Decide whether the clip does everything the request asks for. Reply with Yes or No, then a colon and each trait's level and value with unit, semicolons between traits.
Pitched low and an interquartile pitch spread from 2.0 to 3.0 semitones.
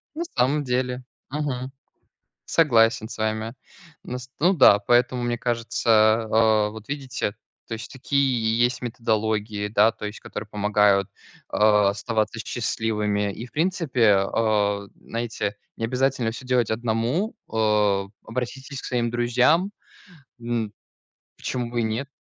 Yes: low, 115 Hz; average, 2.7 semitones